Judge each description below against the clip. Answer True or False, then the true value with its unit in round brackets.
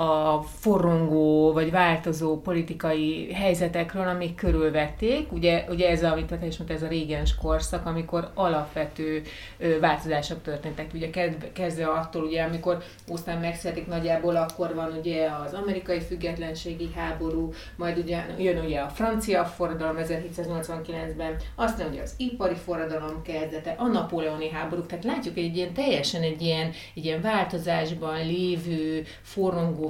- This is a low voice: False (165 Hz)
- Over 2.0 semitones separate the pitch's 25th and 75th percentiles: False (1.6 semitones)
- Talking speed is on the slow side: False (130 wpm)